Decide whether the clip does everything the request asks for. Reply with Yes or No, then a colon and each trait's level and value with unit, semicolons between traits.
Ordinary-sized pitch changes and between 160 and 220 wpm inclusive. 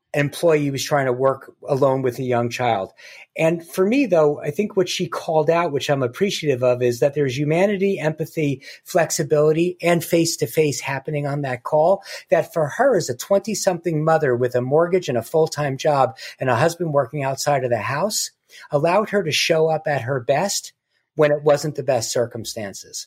Yes: average, 3.5 semitones; average, 200 wpm